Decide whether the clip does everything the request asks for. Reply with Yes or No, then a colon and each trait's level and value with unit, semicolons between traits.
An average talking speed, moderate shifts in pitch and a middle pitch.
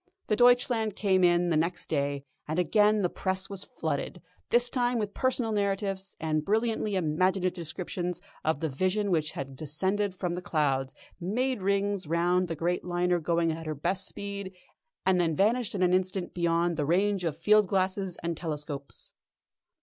Yes: average, 170 wpm; average, 3.4 semitones; medium, 180 Hz